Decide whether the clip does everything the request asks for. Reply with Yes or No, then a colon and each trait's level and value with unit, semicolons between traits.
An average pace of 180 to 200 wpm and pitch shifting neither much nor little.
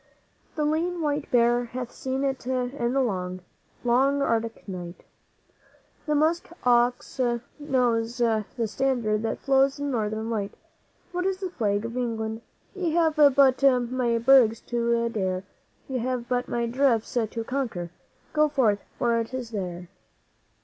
No: average, 145 wpm; average, 3.2 semitones